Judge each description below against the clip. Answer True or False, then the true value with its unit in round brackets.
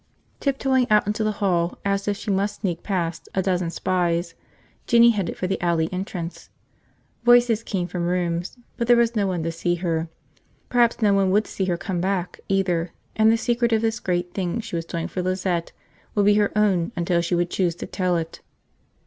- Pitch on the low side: False (185 Hz)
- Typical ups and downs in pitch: True (3.4 semitones)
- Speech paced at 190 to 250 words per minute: True (205 wpm)